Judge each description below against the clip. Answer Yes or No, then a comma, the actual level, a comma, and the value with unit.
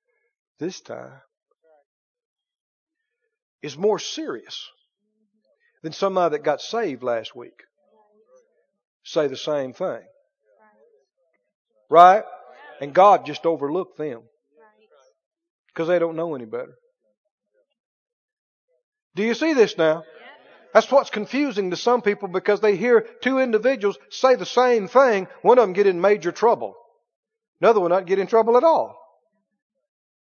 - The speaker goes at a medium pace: No, slow, 125 wpm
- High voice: Yes, high, 220 Hz